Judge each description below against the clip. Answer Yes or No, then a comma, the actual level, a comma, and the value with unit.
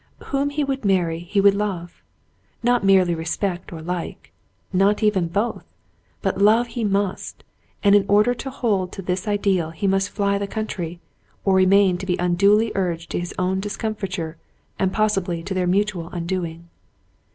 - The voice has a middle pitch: No, high, 195 Hz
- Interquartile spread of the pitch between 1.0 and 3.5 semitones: Yes, average, 2.8 semitones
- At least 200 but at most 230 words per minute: No, average, 175 wpm